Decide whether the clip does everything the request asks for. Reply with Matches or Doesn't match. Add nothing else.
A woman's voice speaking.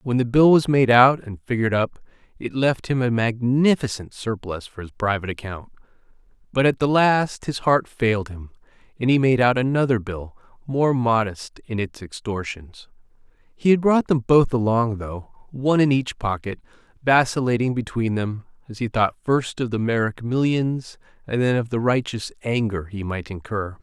Doesn't match